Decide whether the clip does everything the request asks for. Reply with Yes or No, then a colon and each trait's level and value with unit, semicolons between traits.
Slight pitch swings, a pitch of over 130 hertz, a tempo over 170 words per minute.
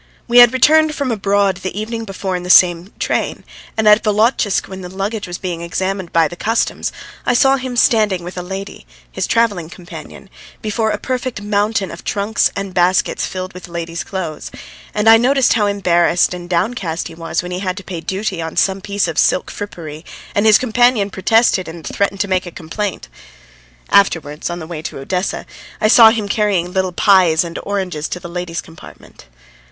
No: average, 3.5 semitones; high, 190 Hz; average, 190 wpm